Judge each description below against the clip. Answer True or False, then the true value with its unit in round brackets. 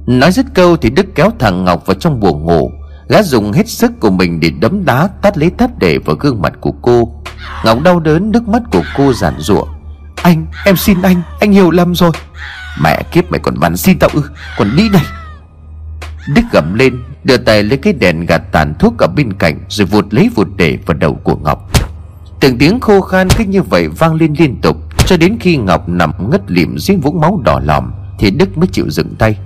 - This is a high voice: False (120 Hz)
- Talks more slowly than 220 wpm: False (225 wpm)